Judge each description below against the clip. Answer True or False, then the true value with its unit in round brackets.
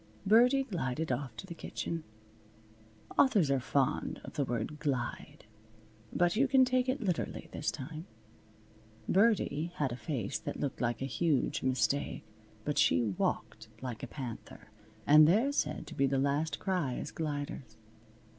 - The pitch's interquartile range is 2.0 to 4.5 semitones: False (5.6 semitones)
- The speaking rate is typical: True (155 wpm)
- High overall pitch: False (150 Hz)